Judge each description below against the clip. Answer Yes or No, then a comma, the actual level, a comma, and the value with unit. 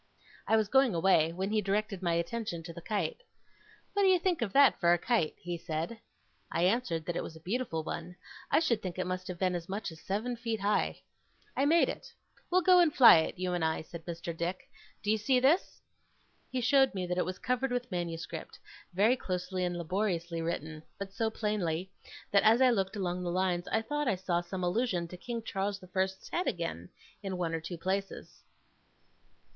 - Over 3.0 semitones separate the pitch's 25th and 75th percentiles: Yes, average, 4.8 semitones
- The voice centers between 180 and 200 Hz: Yes, high, 190 Hz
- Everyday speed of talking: No, fast, 210 wpm